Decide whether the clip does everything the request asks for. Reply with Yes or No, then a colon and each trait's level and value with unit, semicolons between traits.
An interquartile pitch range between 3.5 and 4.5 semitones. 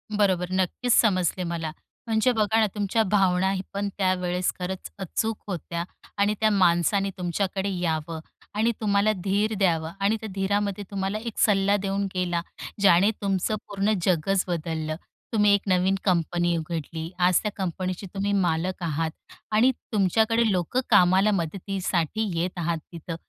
No: average, 2.7 semitones